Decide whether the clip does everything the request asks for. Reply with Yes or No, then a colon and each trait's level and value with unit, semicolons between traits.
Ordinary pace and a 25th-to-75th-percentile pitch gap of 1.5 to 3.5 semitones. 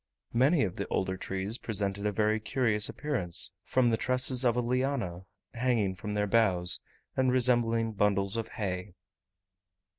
No: average, 150 wpm; average, 4.1 semitones